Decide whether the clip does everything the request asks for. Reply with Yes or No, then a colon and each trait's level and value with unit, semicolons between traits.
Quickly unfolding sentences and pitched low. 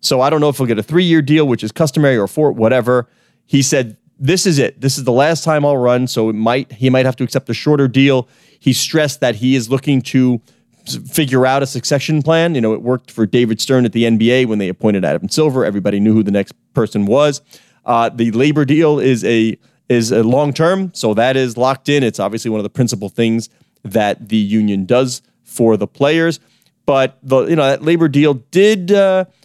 Yes: fast, 230 wpm; low, 130 Hz